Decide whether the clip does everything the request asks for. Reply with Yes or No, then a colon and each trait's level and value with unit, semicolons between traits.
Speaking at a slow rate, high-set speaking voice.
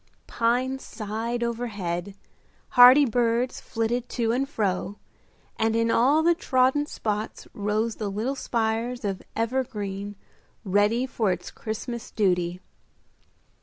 Yes: slow, 115 wpm; high, 230 Hz